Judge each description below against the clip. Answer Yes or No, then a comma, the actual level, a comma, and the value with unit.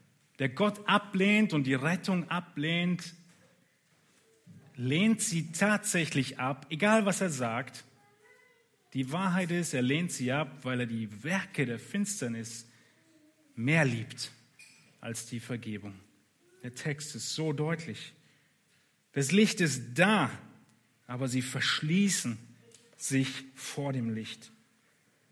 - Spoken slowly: Yes, slow, 115 wpm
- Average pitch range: No, wide, 6.3 semitones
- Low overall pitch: No, medium, 145 Hz